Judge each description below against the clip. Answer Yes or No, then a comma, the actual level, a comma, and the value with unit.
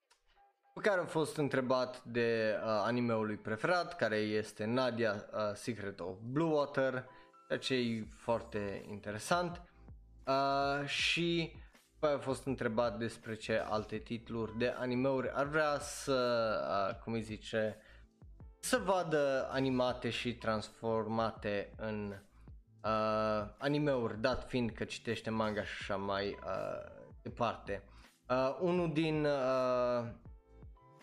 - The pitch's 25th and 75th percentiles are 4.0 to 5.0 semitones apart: Yes, average, 4.4 semitones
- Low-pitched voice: Yes, low, 120 Hz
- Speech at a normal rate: Yes, average, 125 wpm